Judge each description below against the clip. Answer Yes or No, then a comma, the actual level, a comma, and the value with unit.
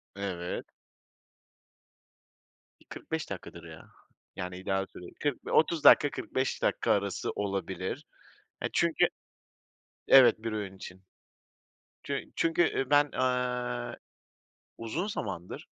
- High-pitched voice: No, low, 110 Hz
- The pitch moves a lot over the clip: Yes, wide, 5.7 semitones